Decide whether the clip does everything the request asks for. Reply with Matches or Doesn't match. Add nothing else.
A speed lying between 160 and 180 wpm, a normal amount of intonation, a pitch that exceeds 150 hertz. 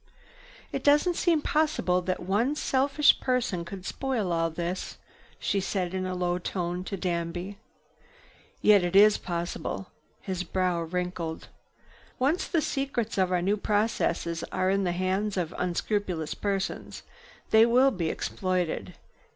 Doesn't match